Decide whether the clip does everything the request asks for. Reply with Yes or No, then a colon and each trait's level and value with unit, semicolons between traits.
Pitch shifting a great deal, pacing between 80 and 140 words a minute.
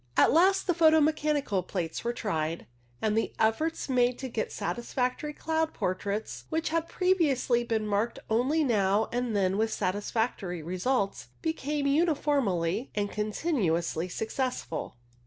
Yes: wide, 6.8 semitones; slow, 135 wpm